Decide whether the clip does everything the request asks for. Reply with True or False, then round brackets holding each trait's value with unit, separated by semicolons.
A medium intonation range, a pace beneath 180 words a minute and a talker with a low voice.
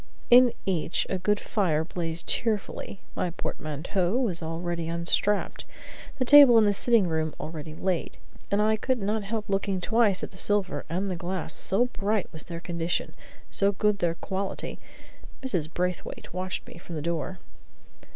False (3.6 semitones; 160 wpm; 185 Hz)